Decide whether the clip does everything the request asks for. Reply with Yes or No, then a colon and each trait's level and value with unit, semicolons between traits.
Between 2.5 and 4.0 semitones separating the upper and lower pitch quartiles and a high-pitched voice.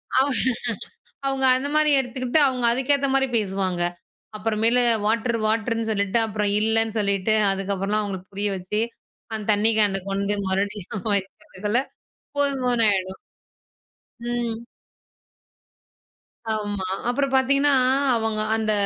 Yes: average, 3.7 semitones; high, 220 Hz